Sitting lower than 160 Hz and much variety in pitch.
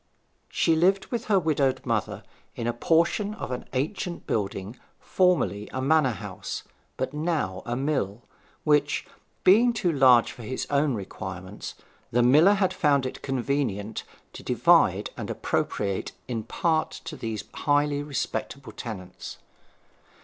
Yes: low, 135 Hz; wide, 5.7 semitones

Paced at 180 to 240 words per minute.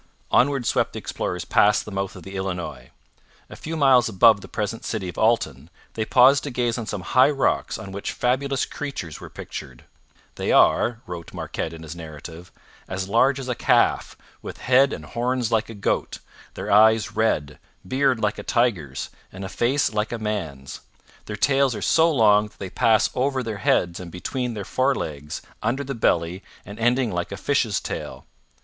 Yes: average, 185 wpm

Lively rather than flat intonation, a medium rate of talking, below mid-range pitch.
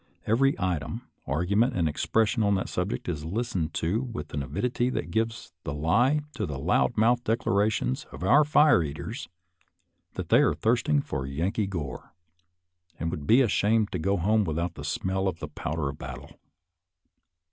Yes: wide, 6.3 semitones; average, 170 wpm; very low, 95 Hz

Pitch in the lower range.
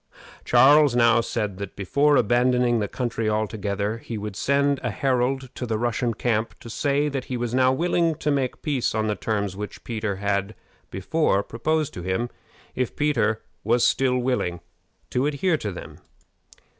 Yes: low, 120 Hz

